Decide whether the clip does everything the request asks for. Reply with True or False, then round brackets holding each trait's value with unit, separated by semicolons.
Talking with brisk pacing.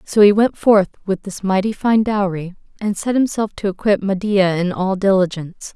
False (190 wpm)